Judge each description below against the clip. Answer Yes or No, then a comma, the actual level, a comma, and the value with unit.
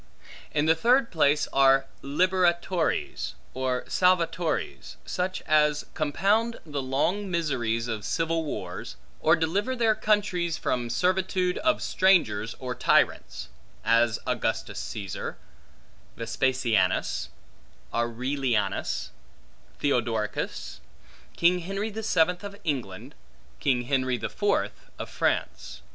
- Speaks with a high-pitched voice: No, medium, 155 Hz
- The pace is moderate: No, slow, 105 wpm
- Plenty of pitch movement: Yes, wide, 6.9 semitones